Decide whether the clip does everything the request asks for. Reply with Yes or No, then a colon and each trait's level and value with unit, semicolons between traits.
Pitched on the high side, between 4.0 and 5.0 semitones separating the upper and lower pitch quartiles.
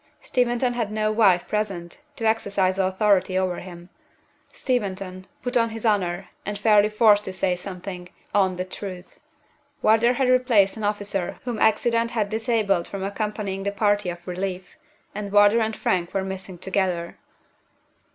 No: high, 200 Hz; average, 2.8 semitones